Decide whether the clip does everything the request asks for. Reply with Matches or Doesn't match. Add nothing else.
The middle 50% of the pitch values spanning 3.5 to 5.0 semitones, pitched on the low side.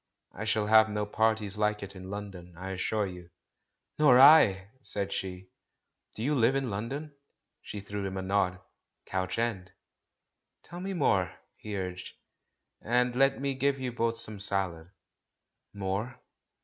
Matches